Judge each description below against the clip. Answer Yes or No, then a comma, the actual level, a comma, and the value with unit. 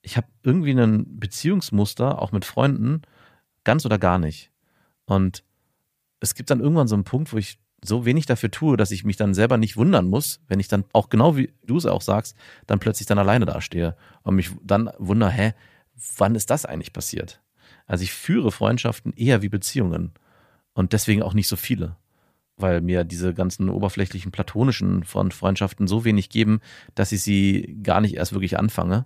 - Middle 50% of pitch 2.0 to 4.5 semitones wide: Yes, average, 3.4 semitones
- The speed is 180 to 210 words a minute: Yes, fast, 190 wpm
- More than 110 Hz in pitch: No, low, 105 Hz